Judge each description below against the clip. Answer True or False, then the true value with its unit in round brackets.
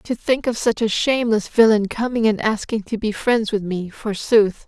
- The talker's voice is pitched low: False (220 Hz)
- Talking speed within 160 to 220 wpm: True (205 wpm)